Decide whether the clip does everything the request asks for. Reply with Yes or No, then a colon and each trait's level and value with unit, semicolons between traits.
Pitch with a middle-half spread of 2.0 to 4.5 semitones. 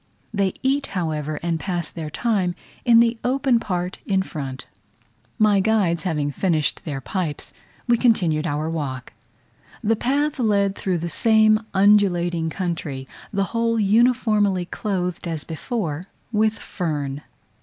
No: average, 5.3 semitones